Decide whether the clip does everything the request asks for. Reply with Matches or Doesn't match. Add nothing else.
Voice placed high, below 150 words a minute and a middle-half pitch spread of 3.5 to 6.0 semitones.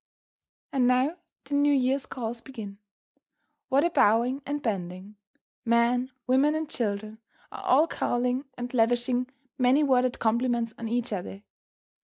Doesn't match